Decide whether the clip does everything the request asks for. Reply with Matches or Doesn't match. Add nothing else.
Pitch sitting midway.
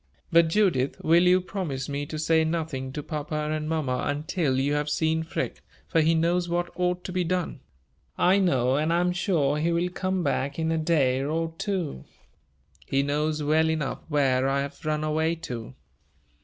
Matches